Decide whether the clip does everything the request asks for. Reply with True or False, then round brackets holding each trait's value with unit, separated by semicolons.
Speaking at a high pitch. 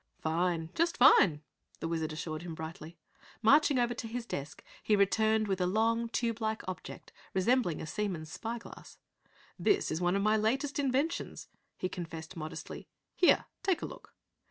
True (205 Hz)